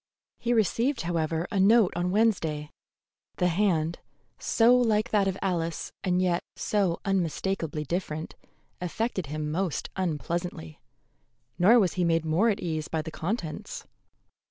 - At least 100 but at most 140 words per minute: Yes, slow, 135 wpm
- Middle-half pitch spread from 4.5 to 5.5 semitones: No, average, 3.9 semitones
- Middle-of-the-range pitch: Yes, medium, 180 Hz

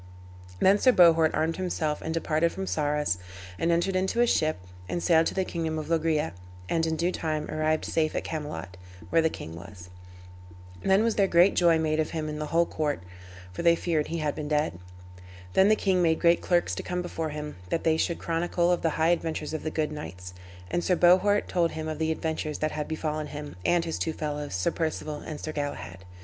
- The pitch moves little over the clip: Yes, narrow, 2.1 semitones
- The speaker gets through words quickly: Yes, fast, 215 wpm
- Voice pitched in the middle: Yes, medium, 160 Hz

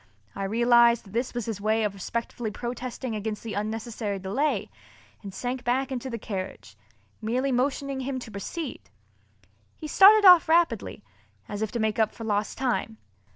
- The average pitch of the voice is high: Yes, high, 235 Hz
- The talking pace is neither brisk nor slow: Yes, average, 165 wpm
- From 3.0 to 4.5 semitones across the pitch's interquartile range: Yes, average, 3.4 semitones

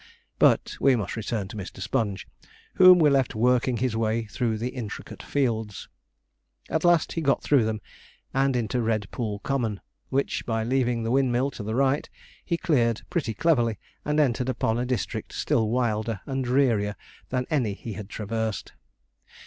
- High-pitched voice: No, low, 120 Hz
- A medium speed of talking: Yes, average, 165 wpm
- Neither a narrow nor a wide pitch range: Yes, average, 3.4 semitones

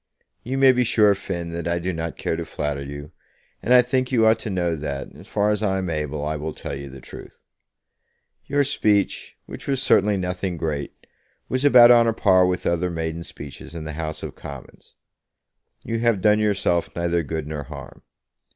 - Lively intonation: Yes, wide, 5.8 semitones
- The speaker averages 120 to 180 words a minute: No, average, 200 wpm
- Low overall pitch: Yes, very low, 90 Hz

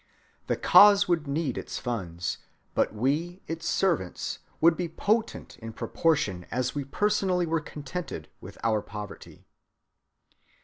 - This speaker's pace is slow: Yes, slow, 130 wpm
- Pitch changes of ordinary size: No, wide, 7.6 semitones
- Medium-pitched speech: Yes, medium, 155 Hz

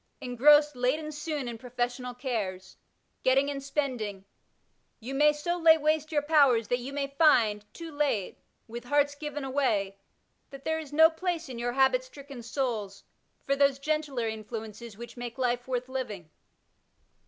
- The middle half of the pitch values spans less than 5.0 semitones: Yes, average, 3.8 semitones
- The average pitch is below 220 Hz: No, very high, 265 Hz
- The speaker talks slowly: No, average, 155 wpm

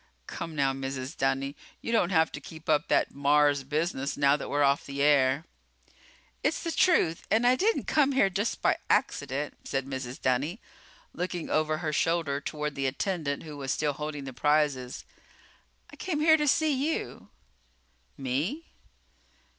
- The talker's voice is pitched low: No, medium, 150 Hz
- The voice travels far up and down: No, average, 4.4 semitones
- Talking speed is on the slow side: No, average, 160 wpm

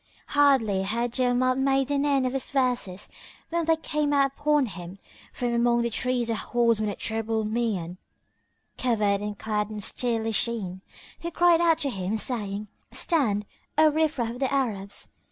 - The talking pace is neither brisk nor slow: Yes, average, 170 wpm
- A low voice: No, high, 240 Hz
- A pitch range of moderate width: Yes, average, 4.7 semitones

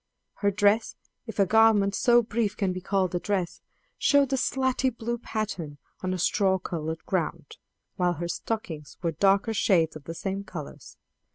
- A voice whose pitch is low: No, high, 195 Hz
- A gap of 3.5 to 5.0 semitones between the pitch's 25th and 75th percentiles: Yes, average, 4.2 semitones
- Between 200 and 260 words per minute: No, average, 170 wpm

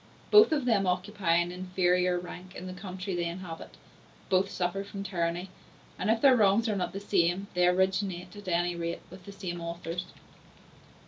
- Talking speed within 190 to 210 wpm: No, average, 180 wpm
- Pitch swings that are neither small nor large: No, narrow, 2.0 semitones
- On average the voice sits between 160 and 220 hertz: Yes, medium, 185 Hz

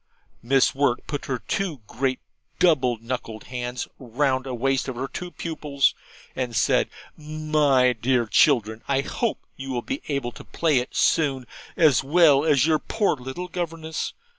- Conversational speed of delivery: Yes, average, 160 wpm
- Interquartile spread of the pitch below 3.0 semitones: No, average, 3.6 semitones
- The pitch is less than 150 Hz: Yes, low, 135 Hz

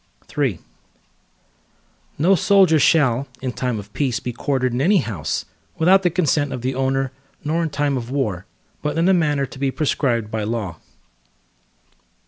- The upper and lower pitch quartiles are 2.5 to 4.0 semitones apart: No, average, 4.5 semitones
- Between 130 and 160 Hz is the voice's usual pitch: Yes, low, 135 Hz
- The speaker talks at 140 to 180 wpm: Yes, average, 160 wpm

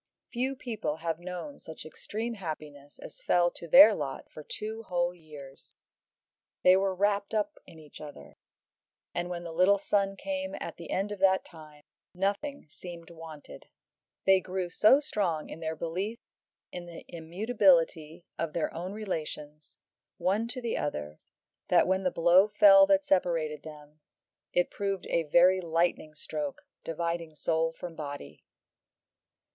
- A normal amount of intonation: Yes, average, 4.2 semitones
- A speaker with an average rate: Yes, average, 150 wpm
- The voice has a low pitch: No, medium, 175 Hz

